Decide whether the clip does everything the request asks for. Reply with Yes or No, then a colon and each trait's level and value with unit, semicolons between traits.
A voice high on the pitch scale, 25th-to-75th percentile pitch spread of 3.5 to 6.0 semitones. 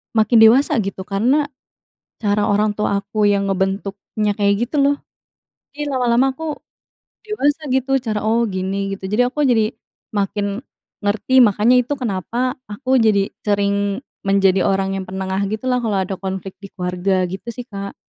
Yes: high, 205 Hz; average, 4.0 semitones